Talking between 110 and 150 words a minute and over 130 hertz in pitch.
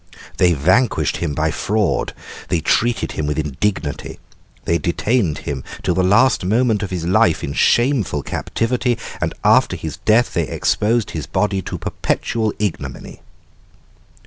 No: average, 145 wpm; very low, 95 Hz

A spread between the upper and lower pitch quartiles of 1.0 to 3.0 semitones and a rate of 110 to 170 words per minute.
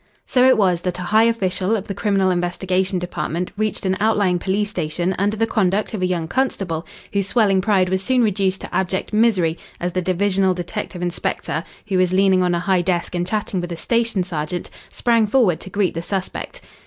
No: average, 2.7 semitones; fast, 205 wpm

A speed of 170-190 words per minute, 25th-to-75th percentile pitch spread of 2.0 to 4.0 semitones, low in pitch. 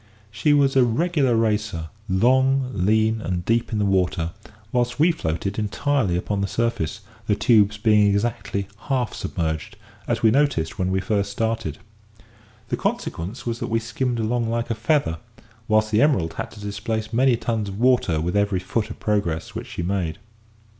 Yes: average, 175 wpm; average, 3.5 semitones; low, 110 Hz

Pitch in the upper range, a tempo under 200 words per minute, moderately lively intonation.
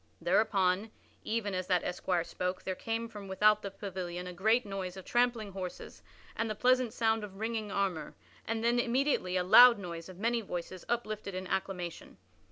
Yes: high, 200 Hz; average, 175 wpm; average, 3.6 semitones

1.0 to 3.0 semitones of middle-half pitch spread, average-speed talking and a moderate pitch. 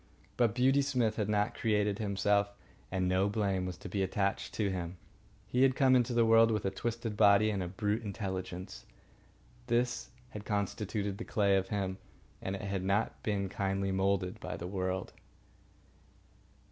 No: narrow, 2.5 semitones; average, 170 wpm; low, 100 Hz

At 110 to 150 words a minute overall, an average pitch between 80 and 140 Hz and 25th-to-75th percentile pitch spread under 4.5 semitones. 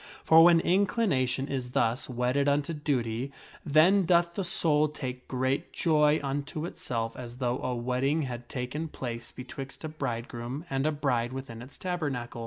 No: average, 160 wpm; low, 135 Hz; average, 3.8 semitones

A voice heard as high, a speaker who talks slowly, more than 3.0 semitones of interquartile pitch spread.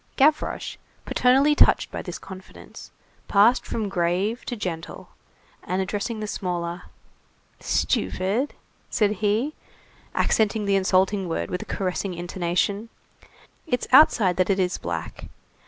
Yes: high, 195 Hz; slow, 120 wpm; average, 3.5 semitones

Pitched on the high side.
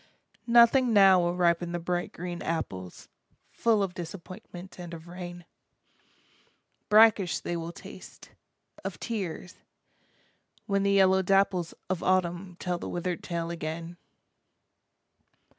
No: medium, 180 Hz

